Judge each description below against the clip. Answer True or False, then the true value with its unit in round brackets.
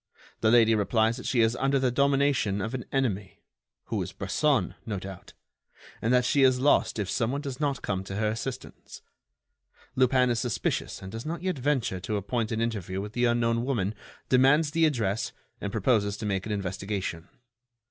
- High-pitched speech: False (115 Hz)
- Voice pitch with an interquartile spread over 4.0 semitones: True (4.5 semitones)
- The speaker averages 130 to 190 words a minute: True (180 wpm)